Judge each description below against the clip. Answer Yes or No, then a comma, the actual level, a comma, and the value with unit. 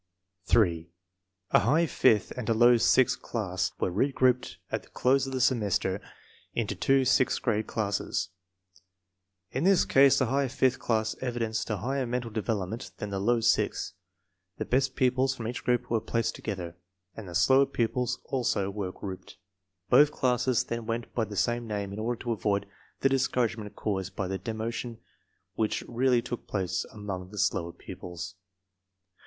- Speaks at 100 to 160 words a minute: No, average, 170 wpm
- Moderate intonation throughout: Yes, average, 3.9 semitones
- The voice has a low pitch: Yes, low, 115 Hz